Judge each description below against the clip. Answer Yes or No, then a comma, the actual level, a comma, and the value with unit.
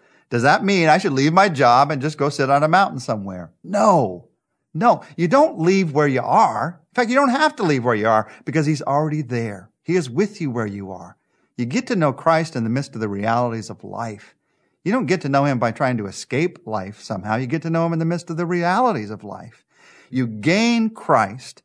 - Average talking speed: No, fast, 240 wpm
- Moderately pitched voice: Yes, medium, 150 Hz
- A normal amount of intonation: No, wide, 7.3 semitones